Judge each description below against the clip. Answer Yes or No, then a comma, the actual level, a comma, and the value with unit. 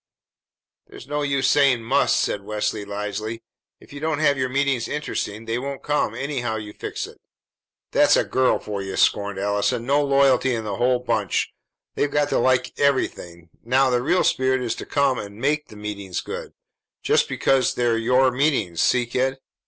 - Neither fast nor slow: Yes, average, 180 wpm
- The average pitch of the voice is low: Yes, low, 125 Hz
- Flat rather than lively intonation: No, average, 4.6 semitones